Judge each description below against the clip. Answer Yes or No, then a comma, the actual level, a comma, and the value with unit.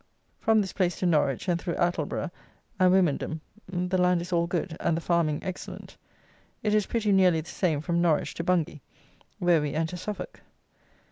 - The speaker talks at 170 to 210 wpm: Yes, average, 180 wpm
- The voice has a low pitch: No, medium, 175 Hz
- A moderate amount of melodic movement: No, narrow, 2.2 semitones